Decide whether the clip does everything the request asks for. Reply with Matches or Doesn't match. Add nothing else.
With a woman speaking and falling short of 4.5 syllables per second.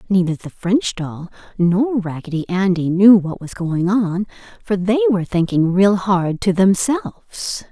Matches